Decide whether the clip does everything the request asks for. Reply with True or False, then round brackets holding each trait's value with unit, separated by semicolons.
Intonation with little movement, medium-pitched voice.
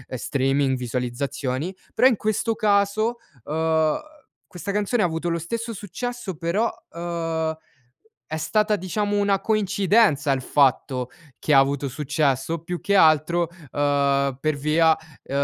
False (6.1 semitones; 165 Hz)